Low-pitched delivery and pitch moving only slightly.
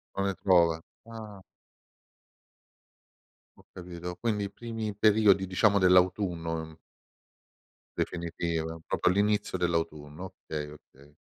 No: very low, 90 Hz; average, 3.6 semitones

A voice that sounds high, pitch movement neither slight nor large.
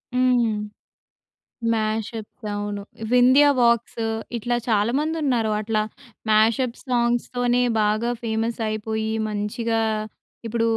No: high, 230 Hz; narrow, 2.2 semitones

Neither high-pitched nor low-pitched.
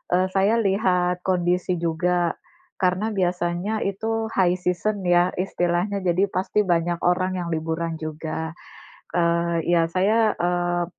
Yes: medium, 180 Hz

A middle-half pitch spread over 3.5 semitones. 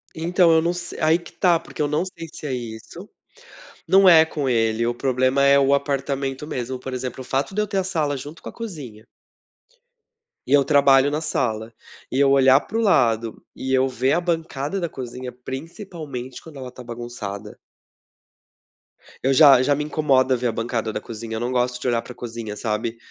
Yes: average, 4.3 semitones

